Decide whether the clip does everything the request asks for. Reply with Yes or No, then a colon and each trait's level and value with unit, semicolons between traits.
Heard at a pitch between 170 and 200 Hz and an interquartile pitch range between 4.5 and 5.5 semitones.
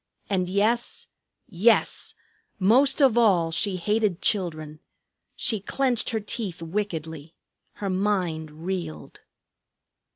Yes: high, 190 Hz; average, 4.8 semitones